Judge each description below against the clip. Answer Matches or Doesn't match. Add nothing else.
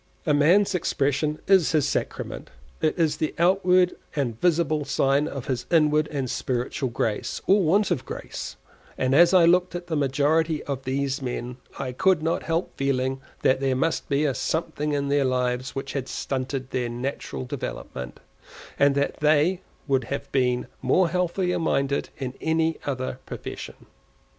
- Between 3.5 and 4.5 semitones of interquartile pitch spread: Matches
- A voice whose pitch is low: Doesn't match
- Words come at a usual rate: Matches